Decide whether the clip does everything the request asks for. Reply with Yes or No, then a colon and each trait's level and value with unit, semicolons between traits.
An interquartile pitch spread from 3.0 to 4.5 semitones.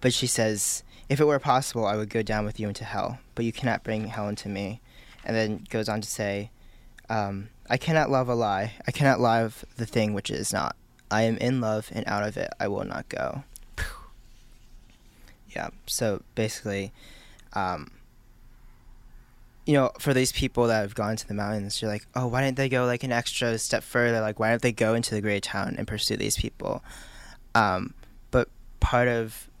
No: narrow, 2.6 semitones